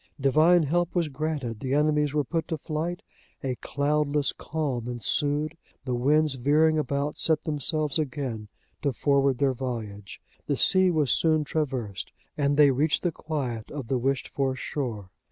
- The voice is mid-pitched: Yes, medium, 145 Hz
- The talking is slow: No, average, 155 wpm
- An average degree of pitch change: Yes, average, 3.0 semitones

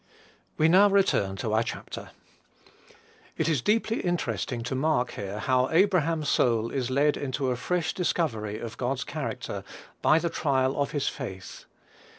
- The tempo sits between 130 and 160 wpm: Yes, average, 155 wpm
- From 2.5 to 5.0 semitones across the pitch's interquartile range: No, wide, 5.5 semitones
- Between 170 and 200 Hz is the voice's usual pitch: No, low, 135 Hz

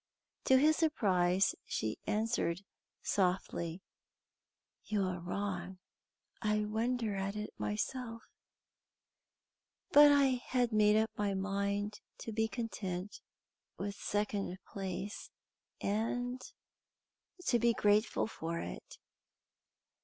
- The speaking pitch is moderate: No, high, 210 Hz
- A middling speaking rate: No, slow, 100 wpm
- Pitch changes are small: No, average, 3.2 semitones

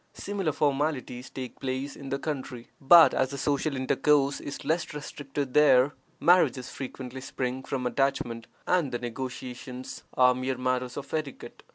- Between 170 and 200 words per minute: No, average, 150 wpm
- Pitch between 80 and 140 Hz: Yes, low, 135 Hz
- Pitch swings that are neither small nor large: No, narrow, 2.3 semitones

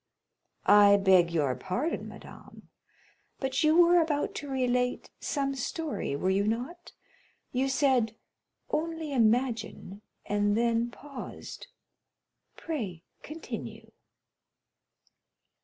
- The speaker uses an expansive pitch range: Yes, wide, 6.1 semitones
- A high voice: Yes, very high, 250 Hz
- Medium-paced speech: No, slow, 90 wpm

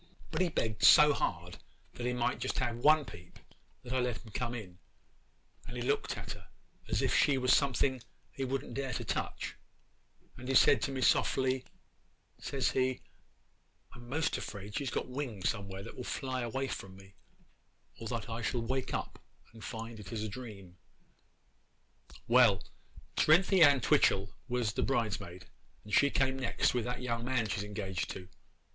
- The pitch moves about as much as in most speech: Yes, average, 3.8 semitones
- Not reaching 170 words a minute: No, average, 180 wpm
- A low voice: Yes, low, 120 Hz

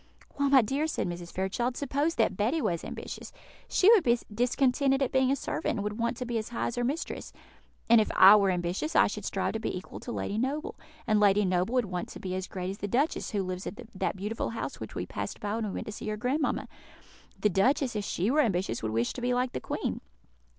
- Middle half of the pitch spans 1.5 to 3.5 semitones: No, average, 5.1 semitones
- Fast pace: Yes, fast, 250 wpm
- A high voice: Yes, high, 225 Hz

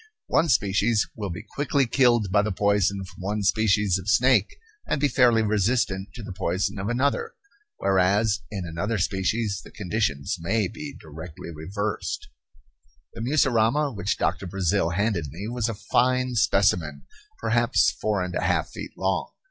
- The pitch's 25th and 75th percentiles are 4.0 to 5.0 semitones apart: No, average, 3.6 semitones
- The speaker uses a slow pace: No, average, 155 wpm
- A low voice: Yes, low, 105 Hz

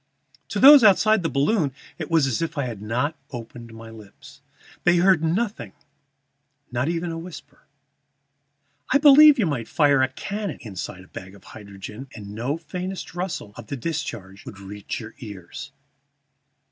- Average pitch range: No, wide, 8.2 semitones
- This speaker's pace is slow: No, average, 160 wpm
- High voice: No, medium, 140 Hz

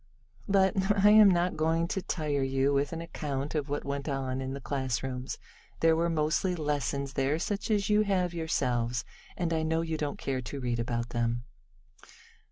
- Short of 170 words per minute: No, average, 180 wpm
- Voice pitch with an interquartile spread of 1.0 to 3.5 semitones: No, average, 4.3 semitones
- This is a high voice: No, medium, 150 Hz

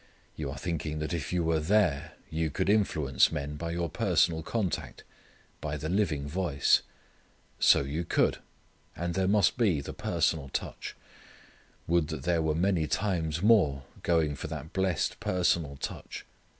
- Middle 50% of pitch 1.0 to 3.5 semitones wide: Yes, average, 3.0 semitones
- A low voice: Yes, very low, 80 Hz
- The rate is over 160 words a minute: No, average, 155 wpm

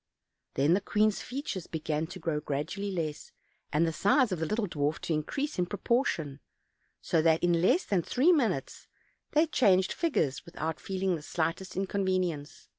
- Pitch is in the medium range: Yes, medium, 180 Hz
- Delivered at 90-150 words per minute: No, average, 165 wpm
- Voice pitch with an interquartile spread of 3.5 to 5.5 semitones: Yes, average, 4.4 semitones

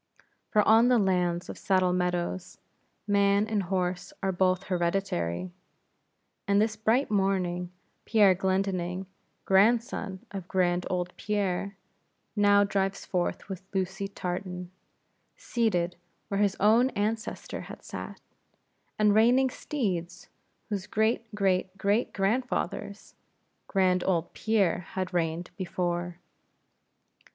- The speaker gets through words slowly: Yes, slow, 110 wpm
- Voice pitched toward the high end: Yes, high, 195 Hz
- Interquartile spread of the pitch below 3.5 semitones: Yes, narrow, 2.6 semitones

